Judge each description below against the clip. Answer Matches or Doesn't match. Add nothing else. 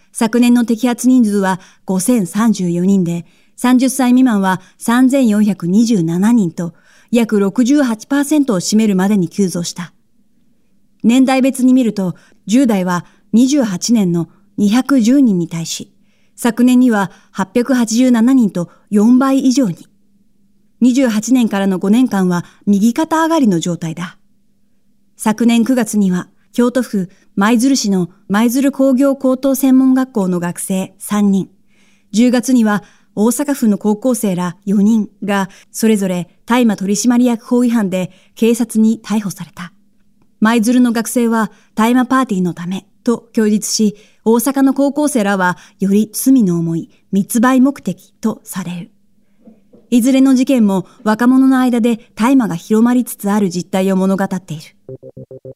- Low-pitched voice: Doesn't match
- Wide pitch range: Doesn't match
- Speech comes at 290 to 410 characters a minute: Doesn't match